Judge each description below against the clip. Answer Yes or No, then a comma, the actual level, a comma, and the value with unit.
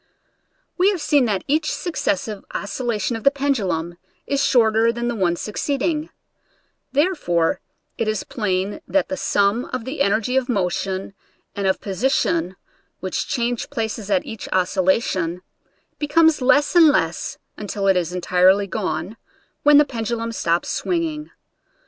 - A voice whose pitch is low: No, high, 225 Hz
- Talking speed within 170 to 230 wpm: No, average, 145 wpm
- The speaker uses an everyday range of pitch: No, wide, 6.8 semitones